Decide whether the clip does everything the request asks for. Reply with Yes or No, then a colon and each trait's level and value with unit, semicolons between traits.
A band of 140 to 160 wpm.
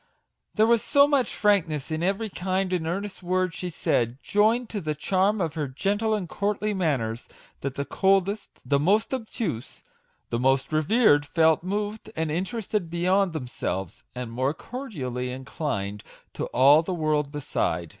Yes: average, 155 wpm